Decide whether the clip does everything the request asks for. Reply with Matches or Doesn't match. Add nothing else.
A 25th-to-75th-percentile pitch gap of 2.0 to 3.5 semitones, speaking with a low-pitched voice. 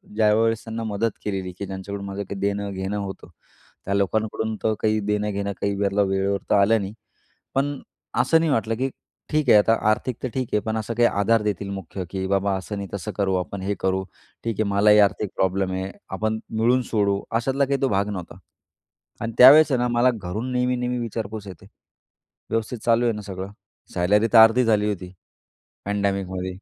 Matches